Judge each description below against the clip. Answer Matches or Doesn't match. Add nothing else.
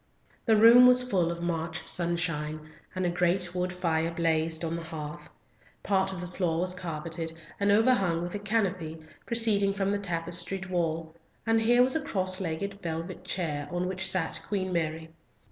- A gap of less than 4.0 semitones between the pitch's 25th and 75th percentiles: Matches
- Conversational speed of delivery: Matches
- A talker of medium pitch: Matches